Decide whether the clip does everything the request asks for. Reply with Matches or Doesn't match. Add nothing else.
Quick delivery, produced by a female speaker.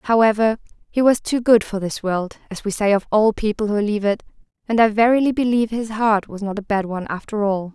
Matches